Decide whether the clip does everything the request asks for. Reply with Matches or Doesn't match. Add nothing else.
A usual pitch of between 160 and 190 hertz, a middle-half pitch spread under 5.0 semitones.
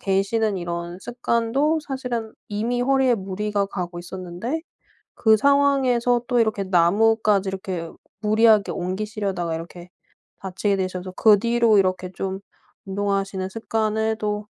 Doesn't match